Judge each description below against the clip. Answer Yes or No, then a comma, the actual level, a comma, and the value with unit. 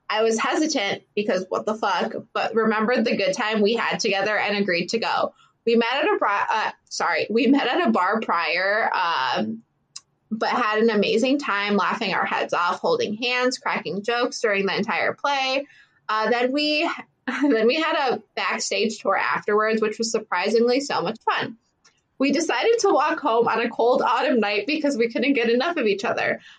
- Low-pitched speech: No, high, 230 Hz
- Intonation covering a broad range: No, average, 4.0 semitones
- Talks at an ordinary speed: Yes, average, 190 wpm